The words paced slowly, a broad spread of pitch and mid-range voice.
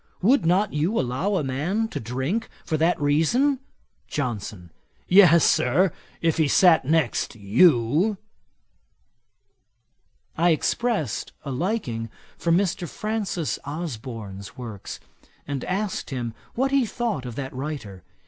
Yes: slow, 120 wpm; wide, 7.3 semitones; medium, 155 Hz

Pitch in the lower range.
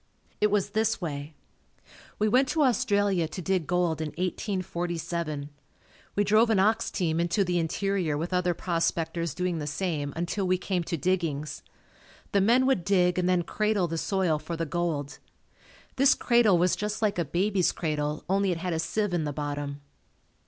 No: medium, 180 Hz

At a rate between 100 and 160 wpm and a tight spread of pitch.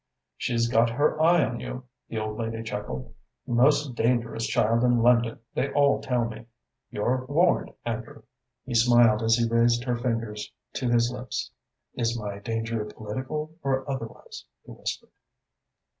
Yes: average, 150 wpm; narrow, 2.1 semitones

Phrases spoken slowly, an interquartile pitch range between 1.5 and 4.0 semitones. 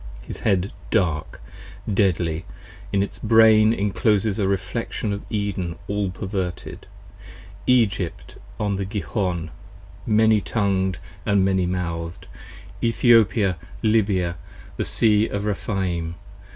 Yes: slow, 110 wpm; average, 2.9 semitones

